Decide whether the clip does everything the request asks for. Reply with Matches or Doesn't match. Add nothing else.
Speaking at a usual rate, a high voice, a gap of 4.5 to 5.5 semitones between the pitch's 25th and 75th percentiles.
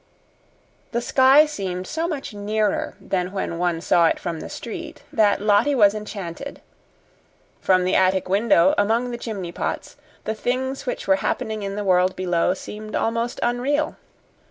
Matches